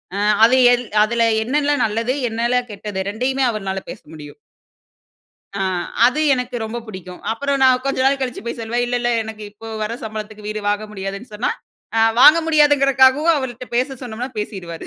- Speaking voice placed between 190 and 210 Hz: No, high, 235 Hz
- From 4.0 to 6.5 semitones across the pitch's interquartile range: No, average, 3.5 semitones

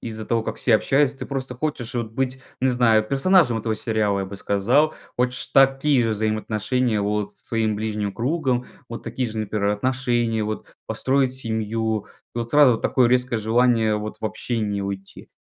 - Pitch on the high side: No, low, 115 Hz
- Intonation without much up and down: No, average, 3.1 semitones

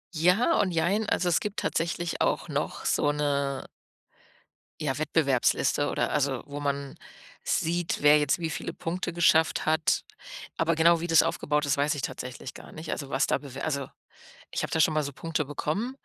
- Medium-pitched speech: Yes, medium, 155 Hz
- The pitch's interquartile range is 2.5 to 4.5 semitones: Yes, average, 2.8 semitones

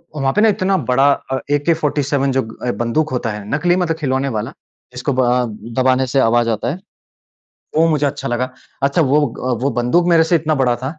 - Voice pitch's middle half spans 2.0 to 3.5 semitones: No, average, 3.9 semitones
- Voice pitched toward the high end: No, low, 135 Hz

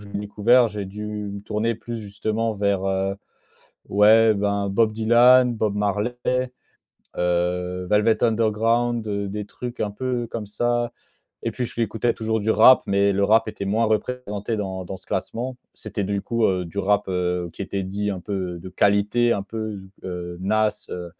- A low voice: Yes, low, 105 Hz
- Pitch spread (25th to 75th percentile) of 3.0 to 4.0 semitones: No, narrow, 2.4 semitones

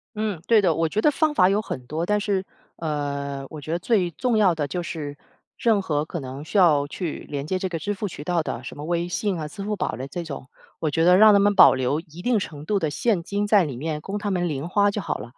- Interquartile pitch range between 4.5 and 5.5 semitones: Yes, average, 5.2 semitones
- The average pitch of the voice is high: No, medium, 170 Hz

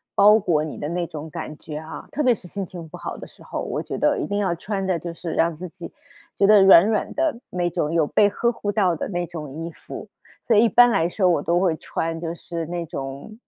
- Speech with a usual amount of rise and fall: Yes, average, 3.8 semitones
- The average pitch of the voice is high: No, medium, 175 Hz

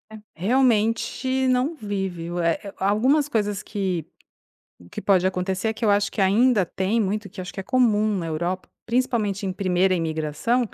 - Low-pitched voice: No, high, 205 Hz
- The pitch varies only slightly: No, average, 3.7 semitones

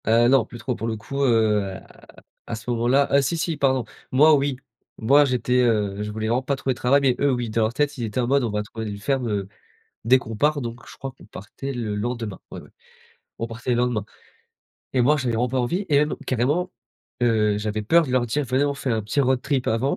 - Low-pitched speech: Yes, low, 125 Hz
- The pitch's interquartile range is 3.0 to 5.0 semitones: Yes, average, 3.6 semitones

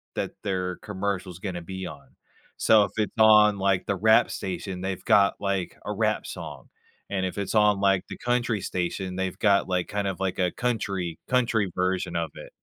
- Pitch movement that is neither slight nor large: No, narrow, 2.2 semitones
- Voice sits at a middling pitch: No, very low, 95 Hz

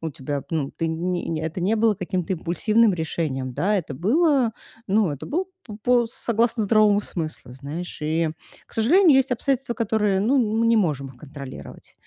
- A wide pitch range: Yes, wide, 6.4 semitones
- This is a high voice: Yes, high, 195 Hz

